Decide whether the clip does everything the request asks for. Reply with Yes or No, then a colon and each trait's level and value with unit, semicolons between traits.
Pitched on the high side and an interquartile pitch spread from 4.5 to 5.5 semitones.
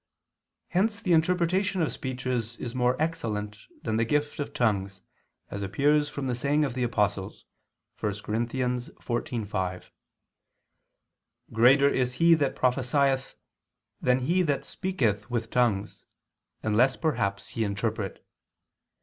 No: low, 125 Hz; average, 5.1 semitones